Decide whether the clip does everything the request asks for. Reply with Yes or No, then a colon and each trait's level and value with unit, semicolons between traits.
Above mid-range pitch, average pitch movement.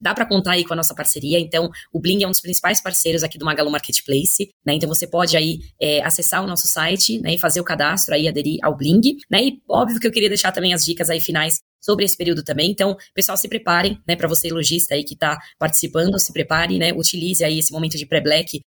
No: medium, 170 Hz; average, 3.0 semitones